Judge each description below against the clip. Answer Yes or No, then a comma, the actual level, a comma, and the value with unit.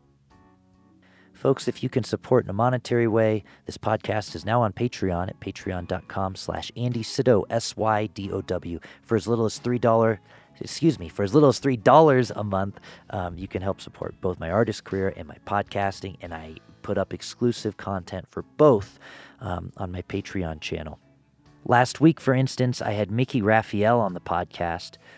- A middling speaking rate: Yes, average, 165 wpm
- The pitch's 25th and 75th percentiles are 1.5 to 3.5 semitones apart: No, average, 4.4 semitones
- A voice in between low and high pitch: No, low, 105 Hz